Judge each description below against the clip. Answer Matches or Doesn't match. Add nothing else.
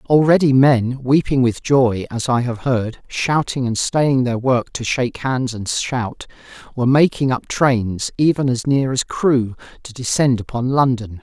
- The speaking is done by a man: Matches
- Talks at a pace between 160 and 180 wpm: Matches